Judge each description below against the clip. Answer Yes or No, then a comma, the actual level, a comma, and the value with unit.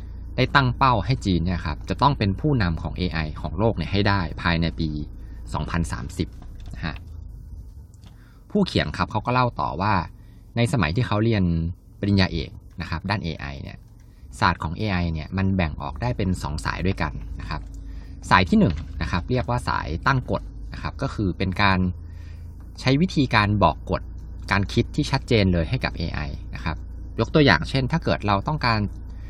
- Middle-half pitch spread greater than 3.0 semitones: Yes, average, 4.6 semitones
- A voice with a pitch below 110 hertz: Yes, very low, 95 Hz